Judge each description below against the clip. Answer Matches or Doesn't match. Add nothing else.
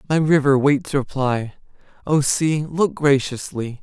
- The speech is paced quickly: Doesn't match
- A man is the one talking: Matches